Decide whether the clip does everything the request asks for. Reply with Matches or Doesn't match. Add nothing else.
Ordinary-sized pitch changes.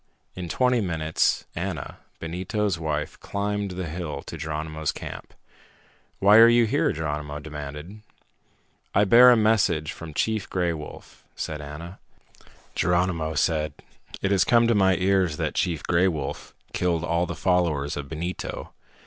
Matches